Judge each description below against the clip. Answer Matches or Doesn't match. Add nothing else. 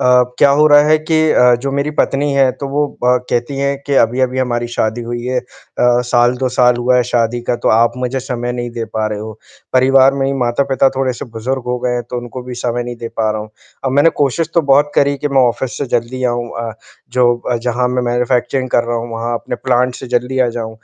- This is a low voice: Matches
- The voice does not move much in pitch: Matches